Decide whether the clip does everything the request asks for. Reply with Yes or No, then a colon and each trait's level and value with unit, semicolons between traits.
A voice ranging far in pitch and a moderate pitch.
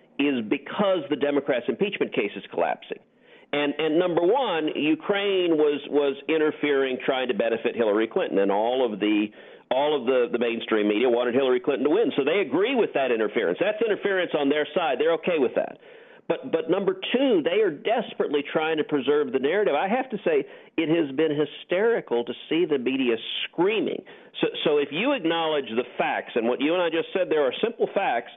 Yes: wide, 8.0 semitones; medium, 150 Hz